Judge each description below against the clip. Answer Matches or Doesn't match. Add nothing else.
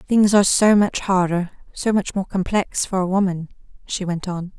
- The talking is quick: Doesn't match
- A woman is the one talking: Matches